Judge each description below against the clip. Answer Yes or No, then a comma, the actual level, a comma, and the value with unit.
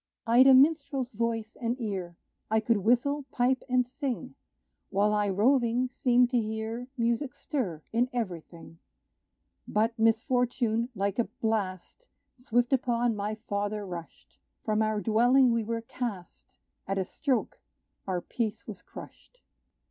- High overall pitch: Yes, high, 230 Hz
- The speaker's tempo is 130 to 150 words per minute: Yes, average, 140 wpm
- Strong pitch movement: No, average, 3.1 semitones